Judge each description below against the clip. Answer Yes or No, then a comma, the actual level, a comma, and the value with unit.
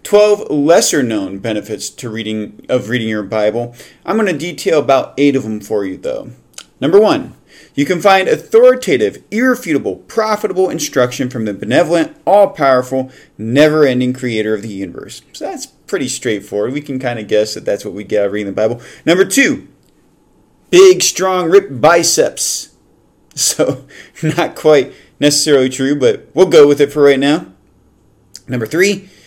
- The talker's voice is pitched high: No, medium, 140 Hz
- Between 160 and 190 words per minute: Yes, average, 165 wpm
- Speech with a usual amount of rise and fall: No, wide, 8.8 semitones